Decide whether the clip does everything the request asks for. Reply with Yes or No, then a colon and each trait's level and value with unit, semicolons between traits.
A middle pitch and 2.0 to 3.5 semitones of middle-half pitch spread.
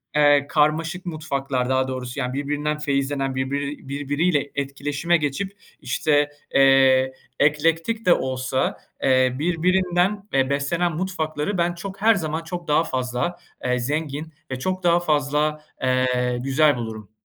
No: medium, 145 Hz; average, 3.9 semitones